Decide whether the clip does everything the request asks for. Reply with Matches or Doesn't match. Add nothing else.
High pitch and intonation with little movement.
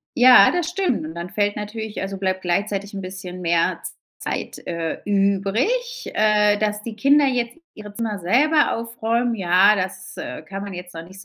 Doesn't match